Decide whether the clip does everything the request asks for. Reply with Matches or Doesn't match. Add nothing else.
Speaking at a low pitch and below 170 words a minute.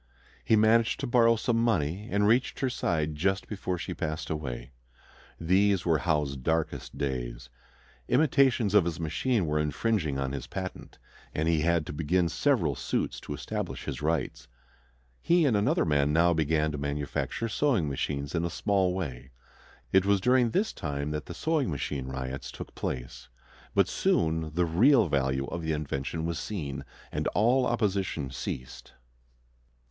Matches